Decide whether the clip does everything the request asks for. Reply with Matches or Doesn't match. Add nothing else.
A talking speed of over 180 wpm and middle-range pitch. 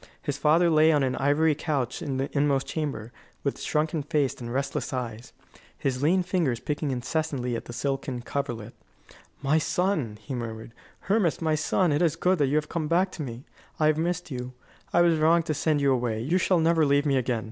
Matches